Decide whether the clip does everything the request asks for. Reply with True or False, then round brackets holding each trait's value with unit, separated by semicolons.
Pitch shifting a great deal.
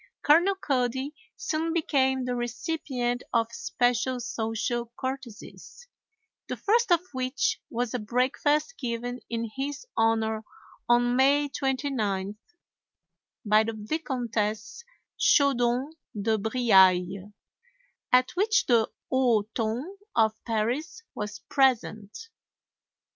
False (3.9 semitones)